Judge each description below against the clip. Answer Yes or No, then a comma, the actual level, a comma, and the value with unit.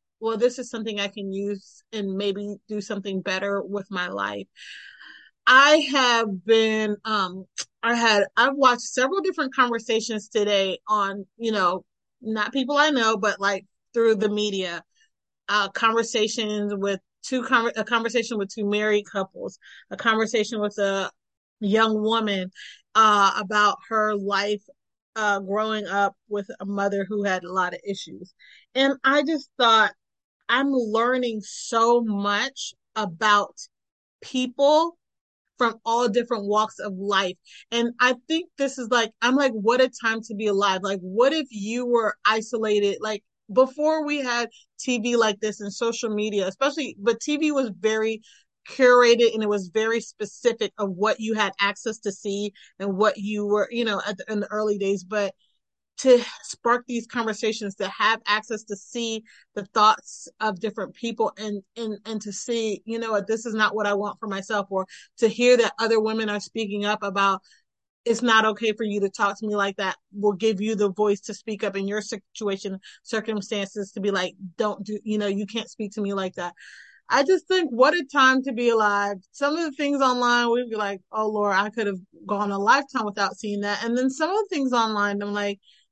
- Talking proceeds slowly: No, average, 185 wpm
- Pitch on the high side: Yes, high, 215 Hz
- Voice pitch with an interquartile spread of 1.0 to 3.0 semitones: Yes, narrow, 2.6 semitones